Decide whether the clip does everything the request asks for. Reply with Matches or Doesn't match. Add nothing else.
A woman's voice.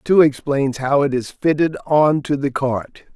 Doesn't match